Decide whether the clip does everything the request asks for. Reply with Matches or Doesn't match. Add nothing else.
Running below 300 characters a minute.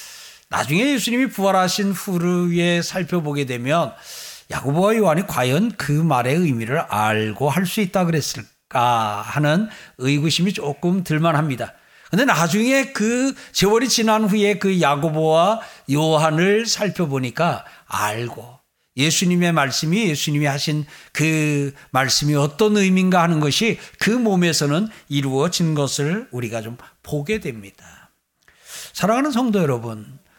Matches